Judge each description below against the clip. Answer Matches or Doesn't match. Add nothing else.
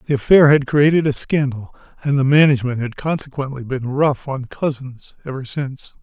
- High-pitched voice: Doesn't match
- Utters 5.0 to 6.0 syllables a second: Matches